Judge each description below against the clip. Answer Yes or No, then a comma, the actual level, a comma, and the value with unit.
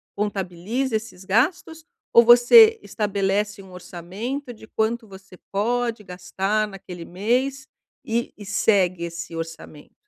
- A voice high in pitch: Yes, high, 210 Hz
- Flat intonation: No, average, 4.3 semitones